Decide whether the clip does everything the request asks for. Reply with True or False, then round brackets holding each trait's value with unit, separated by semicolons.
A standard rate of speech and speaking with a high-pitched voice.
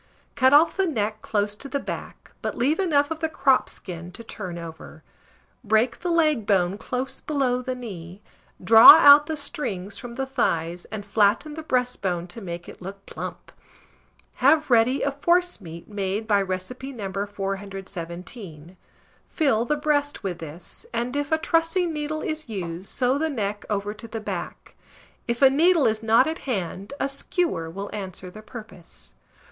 True (170 wpm; 225 Hz)